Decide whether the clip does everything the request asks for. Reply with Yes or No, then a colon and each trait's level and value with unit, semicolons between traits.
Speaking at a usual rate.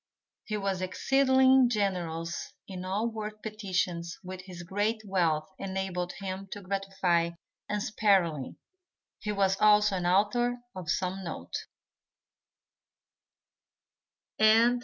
No: slow, 100 wpm